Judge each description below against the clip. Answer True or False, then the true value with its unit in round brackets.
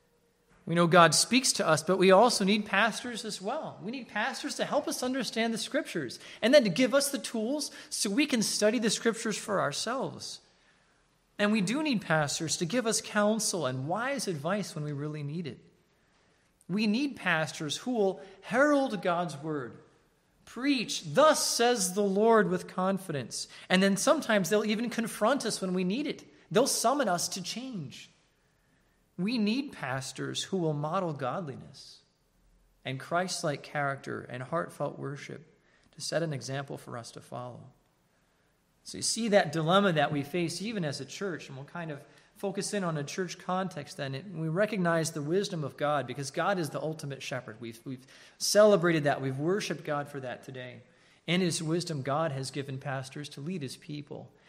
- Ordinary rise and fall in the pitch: False (6.4 semitones)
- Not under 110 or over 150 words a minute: False (180 wpm)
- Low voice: False (180 Hz)